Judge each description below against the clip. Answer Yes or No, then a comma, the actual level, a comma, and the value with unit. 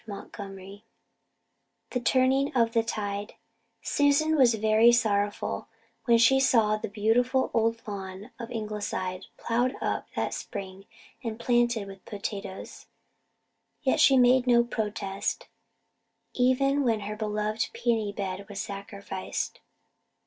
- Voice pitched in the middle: No, high, 220 Hz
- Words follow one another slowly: Yes, slow, 120 wpm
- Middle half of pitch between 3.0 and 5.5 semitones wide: Yes, average, 3.3 semitones